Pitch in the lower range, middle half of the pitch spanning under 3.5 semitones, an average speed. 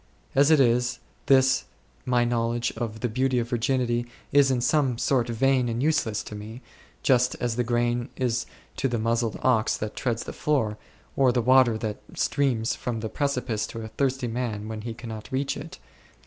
Yes: low, 120 Hz; narrow, 2.4 semitones; average, 190 wpm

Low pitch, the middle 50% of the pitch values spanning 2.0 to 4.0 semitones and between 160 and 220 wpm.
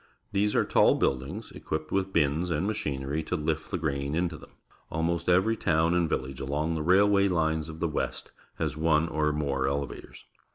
Yes: very low, 80 Hz; average, 3.0 semitones; average, 190 wpm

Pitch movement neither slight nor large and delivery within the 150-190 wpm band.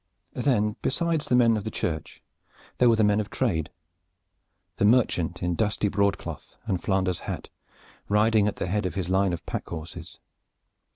Yes: average, 3.6 semitones; average, 170 wpm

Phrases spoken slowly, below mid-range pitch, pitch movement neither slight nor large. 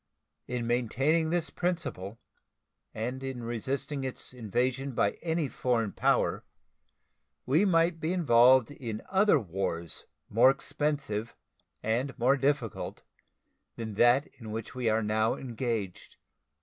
Yes: slow, 120 wpm; low, 125 Hz; average, 4.2 semitones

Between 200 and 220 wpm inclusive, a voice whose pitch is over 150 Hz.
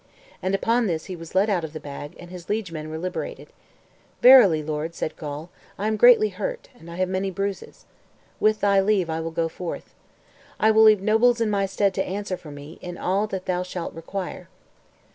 Yes: fast, 205 wpm; medium, 185 Hz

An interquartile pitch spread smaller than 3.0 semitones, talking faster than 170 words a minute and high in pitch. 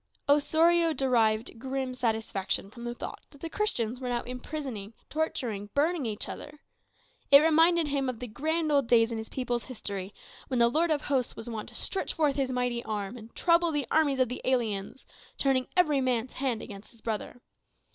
No: average, 4.5 semitones; average, 185 wpm; very high, 255 Hz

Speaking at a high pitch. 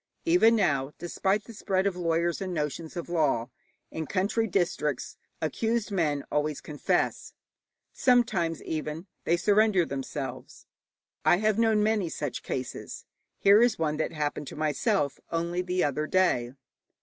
No: medium, 170 Hz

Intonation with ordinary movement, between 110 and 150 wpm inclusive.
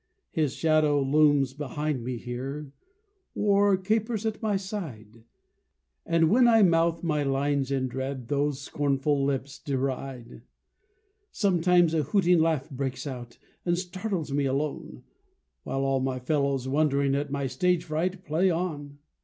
Yes: average, 4.2 semitones; slow, 135 wpm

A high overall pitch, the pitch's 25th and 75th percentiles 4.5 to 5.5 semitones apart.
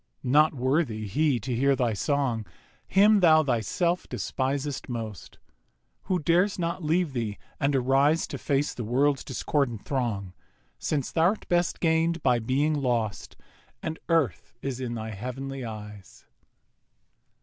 No: low, 135 Hz; average, 5.0 semitones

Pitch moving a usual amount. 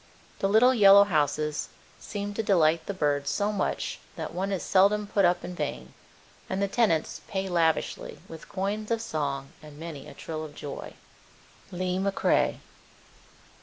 Yes: average, 4.6 semitones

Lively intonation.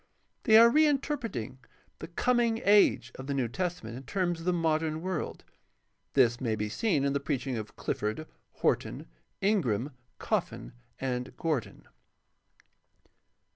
Yes: wide, 7.6 semitones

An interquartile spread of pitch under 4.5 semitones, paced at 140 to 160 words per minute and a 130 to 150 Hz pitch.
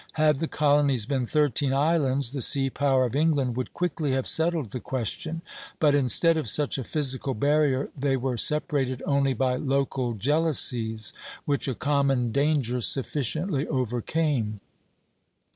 Yes: average, 2.9 semitones; average, 145 wpm; medium, 140 Hz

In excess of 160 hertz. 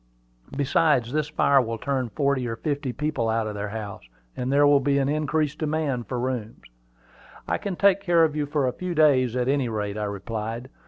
No: low, 135 Hz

